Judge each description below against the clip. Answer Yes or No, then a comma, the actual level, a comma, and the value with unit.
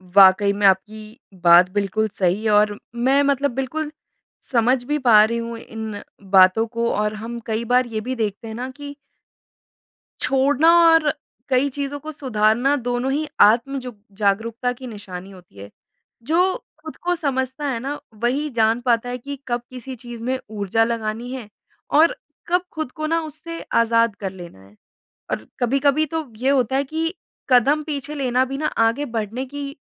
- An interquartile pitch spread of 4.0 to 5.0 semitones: Yes, average, 4.3 semitones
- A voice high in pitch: Yes, high, 245 Hz